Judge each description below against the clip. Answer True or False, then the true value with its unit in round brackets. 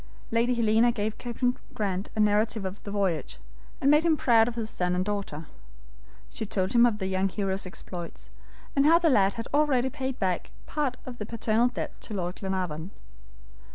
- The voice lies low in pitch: False (215 Hz)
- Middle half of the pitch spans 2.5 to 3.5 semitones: False (4.2 semitones)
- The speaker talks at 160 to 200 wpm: True (190 wpm)